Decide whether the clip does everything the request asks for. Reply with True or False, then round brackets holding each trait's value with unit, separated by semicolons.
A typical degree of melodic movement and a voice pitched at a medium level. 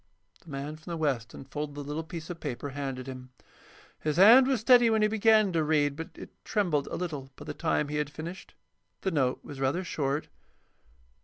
True (4.1 semitones; 150 Hz)